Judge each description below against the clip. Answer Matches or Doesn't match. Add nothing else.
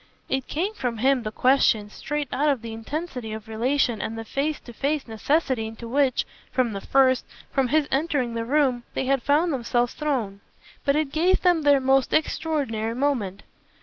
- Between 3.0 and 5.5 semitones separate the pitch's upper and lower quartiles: Matches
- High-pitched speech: Matches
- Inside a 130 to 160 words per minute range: Doesn't match